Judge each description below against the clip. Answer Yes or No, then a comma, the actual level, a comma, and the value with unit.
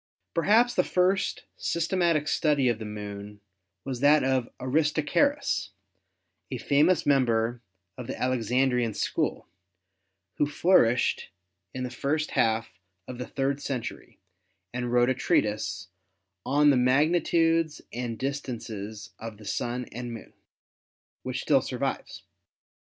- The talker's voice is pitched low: Yes, low, 130 Hz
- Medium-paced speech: No, slow, 125 wpm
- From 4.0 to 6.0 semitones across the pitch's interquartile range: Yes, average, 4.6 semitones